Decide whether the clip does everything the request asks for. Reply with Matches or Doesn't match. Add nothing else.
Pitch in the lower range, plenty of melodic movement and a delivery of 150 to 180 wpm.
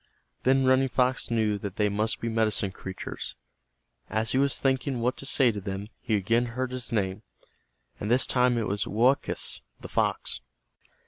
Doesn't match